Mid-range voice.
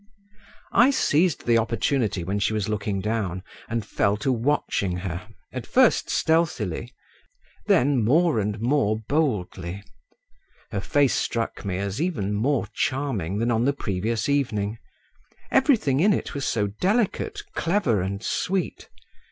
No: low, 115 Hz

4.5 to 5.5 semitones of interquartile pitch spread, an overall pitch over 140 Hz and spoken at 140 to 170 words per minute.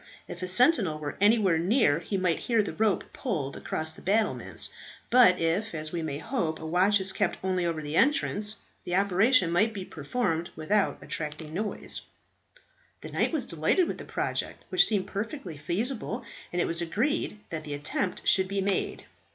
No: average, 4.9 semitones; medium, 185 Hz; average, 180 wpm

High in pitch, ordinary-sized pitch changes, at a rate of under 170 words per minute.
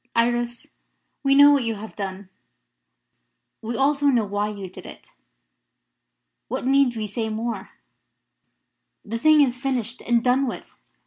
Yes: high, 235 Hz; average, 3.9 semitones; average, 140 wpm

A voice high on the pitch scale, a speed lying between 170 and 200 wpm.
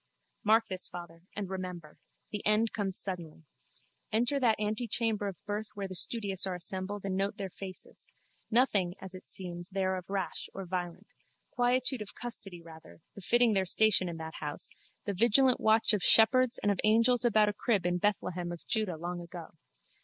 Yes: high, 195 Hz; average, 175 wpm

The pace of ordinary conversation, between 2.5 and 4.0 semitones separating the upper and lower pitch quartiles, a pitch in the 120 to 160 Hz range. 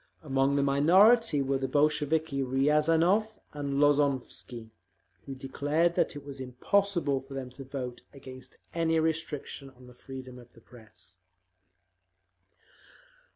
No: slow, 125 wpm; average, 3.0 semitones; medium, 140 Hz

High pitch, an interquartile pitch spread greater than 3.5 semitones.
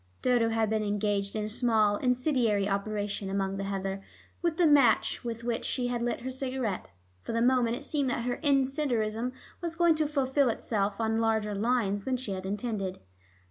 Yes: high, 230 Hz; average, 3.9 semitones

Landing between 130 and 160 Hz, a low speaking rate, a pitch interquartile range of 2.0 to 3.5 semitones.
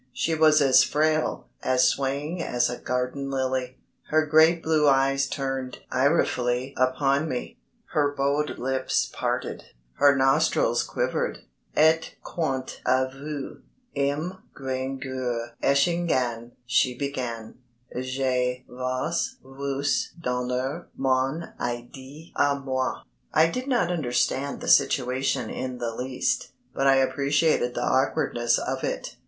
Yes: low, 135 Hz; slow, 120 wpm; narrow, 2.4 semitones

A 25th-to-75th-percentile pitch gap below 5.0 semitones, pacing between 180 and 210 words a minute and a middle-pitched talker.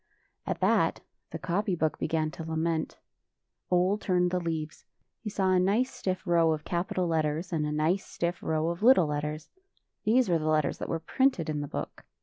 Yes: average, 3.0 semitones; average, 190 wpm; medium, 170 Hz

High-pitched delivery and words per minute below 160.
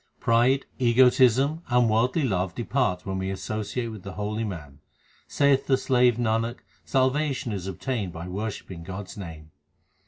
No: low, 110 Hz; average, 145 wpm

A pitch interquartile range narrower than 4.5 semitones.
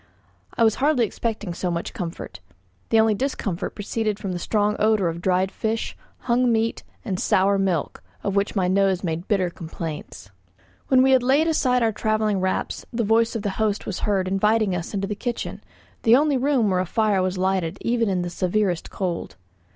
Yes: average, 3.5 semitones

